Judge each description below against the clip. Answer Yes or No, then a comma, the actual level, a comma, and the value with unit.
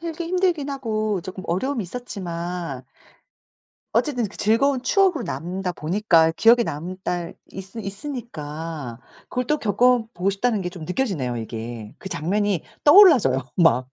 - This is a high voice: Yes, high, 195 Hz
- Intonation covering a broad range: Yes, wide, 6.9 semitones